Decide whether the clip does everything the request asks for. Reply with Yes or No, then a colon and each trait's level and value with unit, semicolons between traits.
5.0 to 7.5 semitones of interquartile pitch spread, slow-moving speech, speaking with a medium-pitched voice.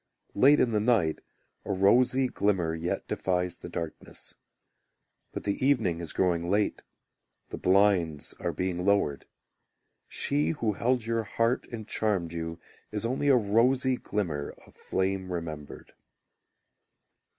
No: average, 5.3 semitones; slow, 130 wpm; low, 100 Hz